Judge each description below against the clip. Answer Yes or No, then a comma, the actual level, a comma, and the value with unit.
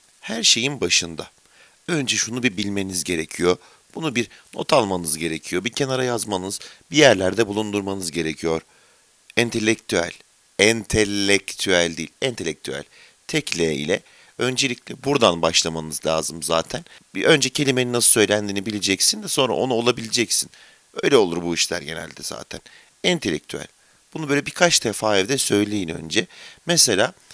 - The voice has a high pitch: No, low, 105 Hz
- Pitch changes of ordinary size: No, wide, 6.3 semitones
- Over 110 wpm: Yes, average, 125 wpm